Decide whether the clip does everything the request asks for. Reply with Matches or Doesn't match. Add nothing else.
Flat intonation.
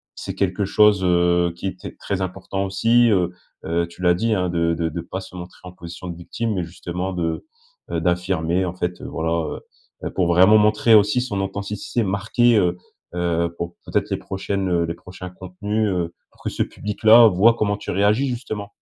Doesn't match